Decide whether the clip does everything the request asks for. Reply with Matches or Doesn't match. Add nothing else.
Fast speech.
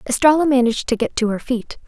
Matches